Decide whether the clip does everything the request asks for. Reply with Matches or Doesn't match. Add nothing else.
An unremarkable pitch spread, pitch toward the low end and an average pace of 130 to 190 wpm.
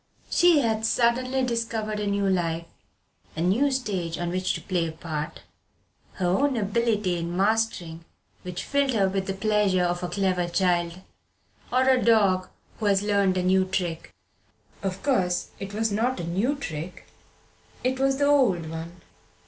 Doesn't match